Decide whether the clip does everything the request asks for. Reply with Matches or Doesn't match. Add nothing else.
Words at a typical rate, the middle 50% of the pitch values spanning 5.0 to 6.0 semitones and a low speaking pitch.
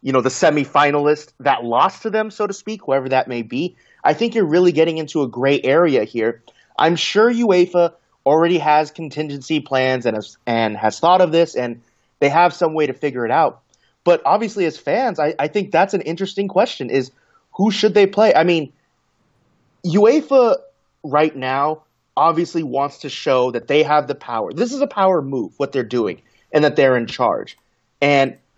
Doesn't match